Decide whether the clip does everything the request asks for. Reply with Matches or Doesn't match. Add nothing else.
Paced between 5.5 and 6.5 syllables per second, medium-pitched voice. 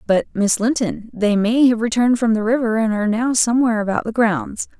Doesn't match